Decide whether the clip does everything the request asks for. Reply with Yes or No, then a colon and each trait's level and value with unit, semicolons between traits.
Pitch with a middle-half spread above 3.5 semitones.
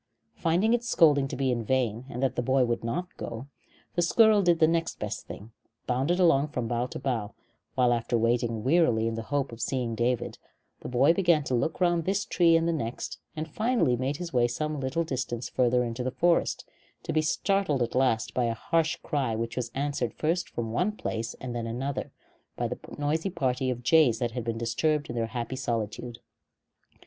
Yes: wide, 5.4 semitones